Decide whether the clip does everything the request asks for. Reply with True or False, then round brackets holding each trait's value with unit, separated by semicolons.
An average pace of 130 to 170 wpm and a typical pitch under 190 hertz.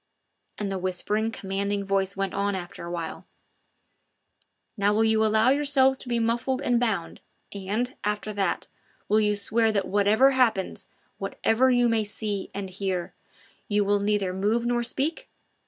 False (155 wpm; 210 Hz)